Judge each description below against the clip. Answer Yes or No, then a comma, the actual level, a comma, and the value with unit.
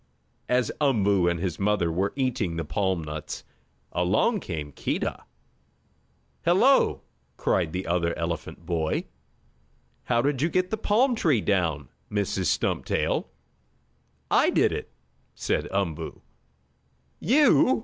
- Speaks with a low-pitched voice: Yes, very low, 95 Hz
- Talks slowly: Yes, slow, 120 wpm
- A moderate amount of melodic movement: No, wide, 8.5 semitones